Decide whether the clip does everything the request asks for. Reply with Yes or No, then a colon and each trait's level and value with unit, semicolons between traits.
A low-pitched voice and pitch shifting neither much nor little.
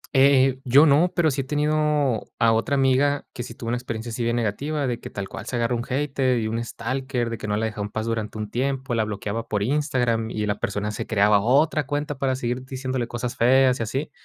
Yes: low, 125 Hz; average, 3.4 semitones